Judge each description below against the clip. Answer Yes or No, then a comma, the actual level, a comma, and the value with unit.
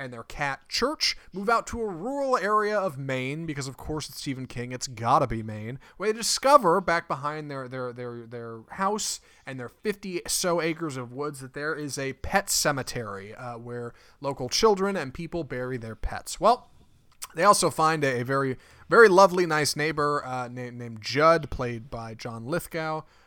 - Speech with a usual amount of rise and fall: No, wide, 5.9 semitones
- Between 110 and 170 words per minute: No, average, 185 wpm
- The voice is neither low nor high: Yes, medium, 145 Hz